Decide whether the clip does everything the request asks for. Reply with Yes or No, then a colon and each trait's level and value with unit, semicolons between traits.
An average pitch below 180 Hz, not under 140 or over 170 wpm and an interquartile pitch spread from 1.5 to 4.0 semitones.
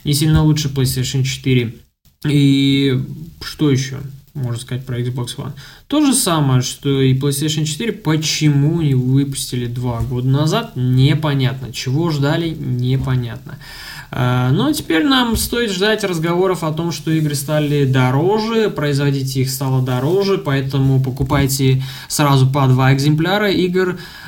No: medium, 140 Hz; average, 130 wpm; average, 3.0 semitones